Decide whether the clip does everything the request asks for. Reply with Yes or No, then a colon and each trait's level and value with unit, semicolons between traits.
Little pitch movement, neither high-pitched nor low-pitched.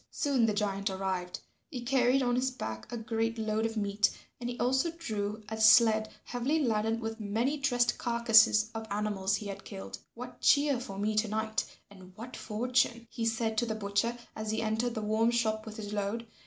No: narrow, 2.3 semitones; high, 220 Hz